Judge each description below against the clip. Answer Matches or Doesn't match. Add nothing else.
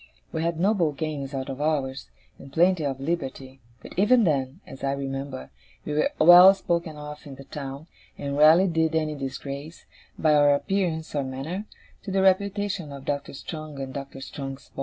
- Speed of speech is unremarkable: Matches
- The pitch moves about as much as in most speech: Matches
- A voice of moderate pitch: Matches